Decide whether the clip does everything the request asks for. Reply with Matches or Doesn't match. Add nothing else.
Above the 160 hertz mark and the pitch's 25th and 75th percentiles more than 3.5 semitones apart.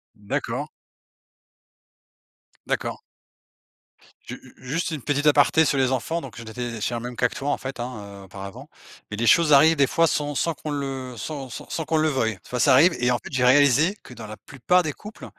Doesn't match